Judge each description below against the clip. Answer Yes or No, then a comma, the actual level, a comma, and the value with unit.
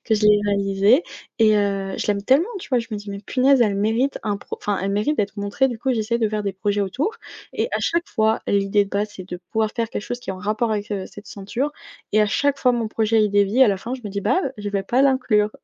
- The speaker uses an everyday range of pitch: Yes, average, 3.1 semitones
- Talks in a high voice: Yes, high, 210 Hz